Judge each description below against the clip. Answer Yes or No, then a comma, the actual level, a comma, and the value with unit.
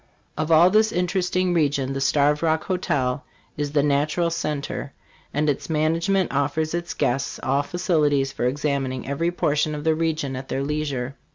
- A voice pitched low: No, medium, 150 Hz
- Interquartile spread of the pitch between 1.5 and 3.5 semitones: Yes, average, 3.0 semitones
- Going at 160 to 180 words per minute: Yes, average, 170 wpm